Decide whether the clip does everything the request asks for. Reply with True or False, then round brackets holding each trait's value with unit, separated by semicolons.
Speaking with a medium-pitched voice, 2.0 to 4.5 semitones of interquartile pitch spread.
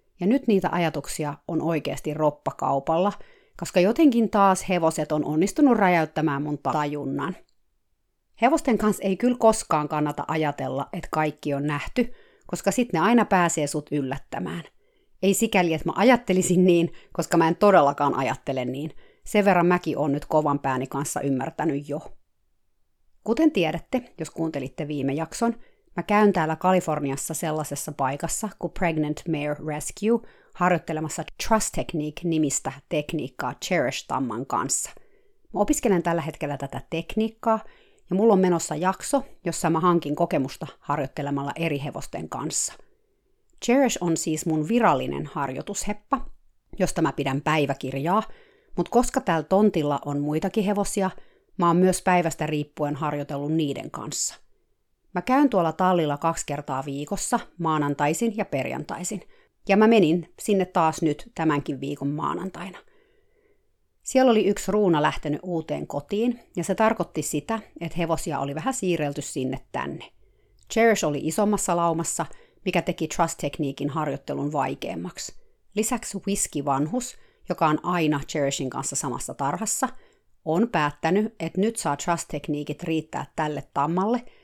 False (165 Hz; 5.4 semitones)